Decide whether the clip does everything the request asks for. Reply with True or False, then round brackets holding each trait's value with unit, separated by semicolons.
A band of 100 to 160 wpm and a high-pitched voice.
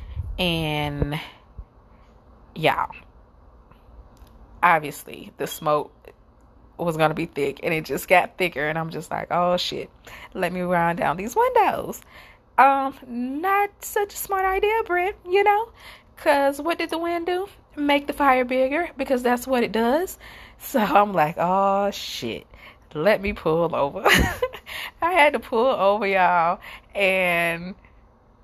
True (140 wpm; 210 Hz)